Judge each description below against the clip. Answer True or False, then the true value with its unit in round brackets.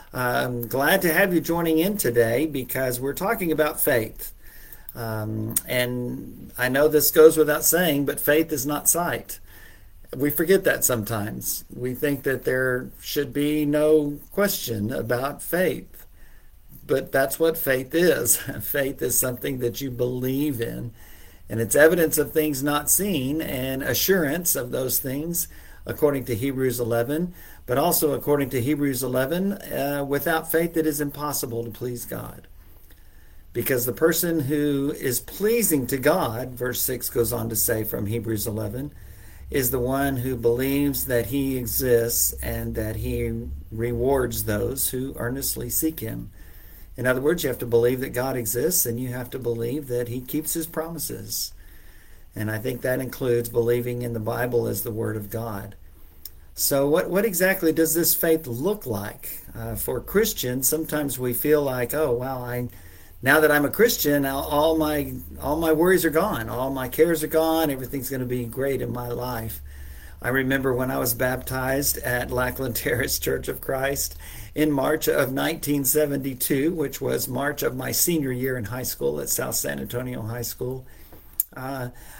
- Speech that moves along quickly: False (165 wpm)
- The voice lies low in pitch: True (130 Hz)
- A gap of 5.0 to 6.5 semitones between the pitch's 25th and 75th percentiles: False (4.2 semitones)